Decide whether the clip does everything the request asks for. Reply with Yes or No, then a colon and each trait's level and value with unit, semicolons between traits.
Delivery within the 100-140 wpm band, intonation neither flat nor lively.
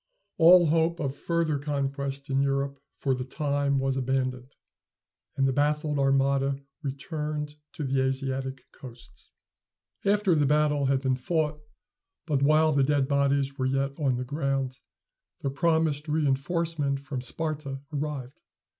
No: slow, 135 wpm; narrow, 2.0 semitones